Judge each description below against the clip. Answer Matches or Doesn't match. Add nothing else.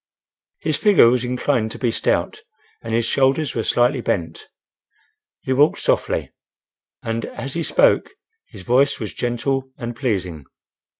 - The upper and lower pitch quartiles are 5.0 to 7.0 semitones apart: Doesn't match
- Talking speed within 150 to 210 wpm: Doesn't match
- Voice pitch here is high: Doesn't match